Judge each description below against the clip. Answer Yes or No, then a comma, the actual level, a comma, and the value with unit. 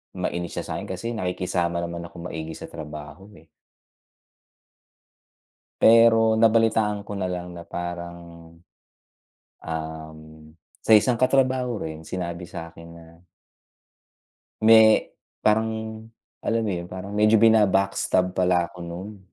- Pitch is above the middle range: No, very low, 90 Hz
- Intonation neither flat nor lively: Yes, average, 4.5 semitones